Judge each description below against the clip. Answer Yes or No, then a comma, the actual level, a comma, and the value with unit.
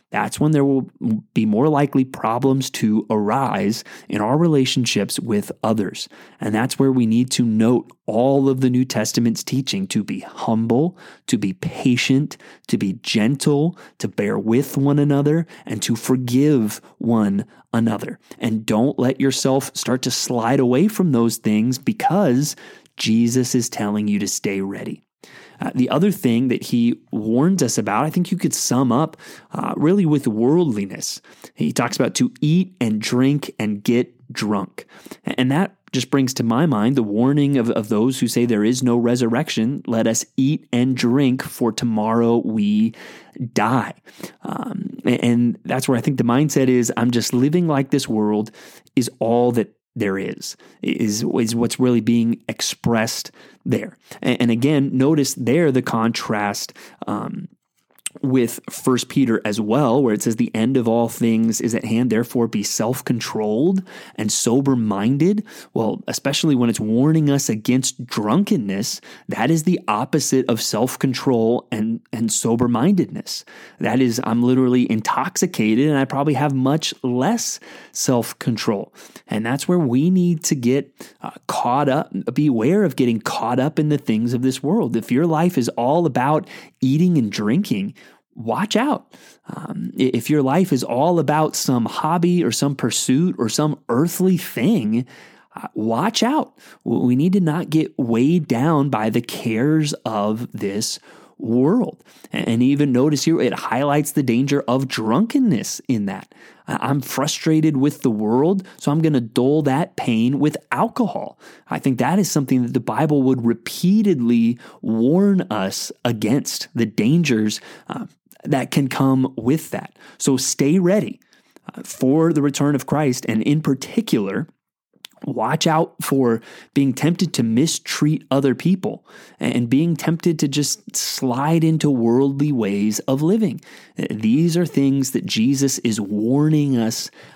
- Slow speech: No, average, 155 wpm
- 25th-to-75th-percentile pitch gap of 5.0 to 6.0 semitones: No, average, 4.5 semitones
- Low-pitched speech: Yes, low, 130 Hz